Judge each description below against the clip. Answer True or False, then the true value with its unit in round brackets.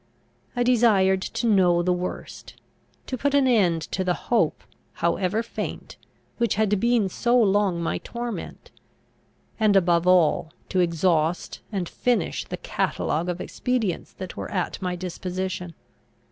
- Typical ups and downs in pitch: True (4.2 semitones)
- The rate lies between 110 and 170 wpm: True (140 wpm)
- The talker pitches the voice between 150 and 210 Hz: True (190 Hz)